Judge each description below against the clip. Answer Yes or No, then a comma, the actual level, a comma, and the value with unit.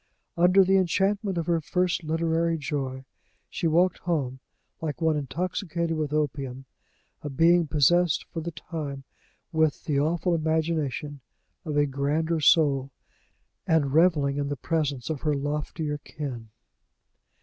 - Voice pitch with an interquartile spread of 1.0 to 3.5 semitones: Yes, average, 2.9 semitones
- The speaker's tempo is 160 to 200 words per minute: No, slow, 135 wpm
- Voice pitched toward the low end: No, medium, 155 Hz